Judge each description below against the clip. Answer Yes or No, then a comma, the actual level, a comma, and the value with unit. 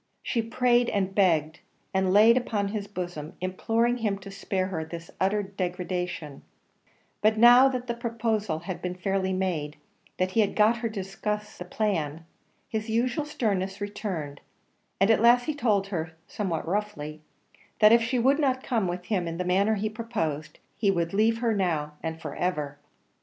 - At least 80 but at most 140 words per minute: No, average, 175 wpm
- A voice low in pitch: No, high, 200 Hz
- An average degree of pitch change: Yes, average, 4.1 semitones